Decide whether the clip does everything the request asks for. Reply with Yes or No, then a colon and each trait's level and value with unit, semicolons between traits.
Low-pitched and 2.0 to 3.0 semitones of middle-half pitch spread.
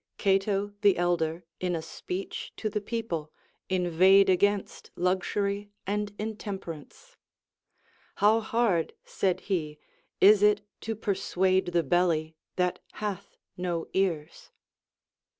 No: high, 190 Hz; average, 2.7 semitones